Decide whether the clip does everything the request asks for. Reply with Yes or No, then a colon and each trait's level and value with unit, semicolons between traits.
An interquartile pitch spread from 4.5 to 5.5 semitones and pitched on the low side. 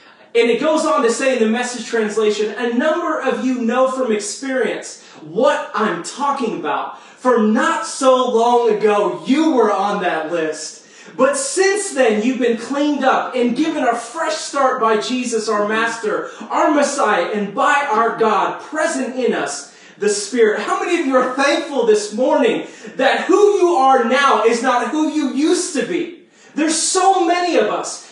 No: average, 5.2 semitones; very high, 255 Hz